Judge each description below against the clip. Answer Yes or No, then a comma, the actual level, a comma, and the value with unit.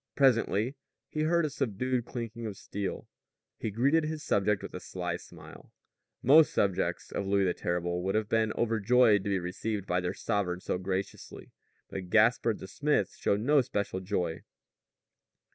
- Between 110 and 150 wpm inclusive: No, average, 160 wpm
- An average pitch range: Yes, average, 4.7 semitones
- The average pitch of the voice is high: No, low, 105 Hz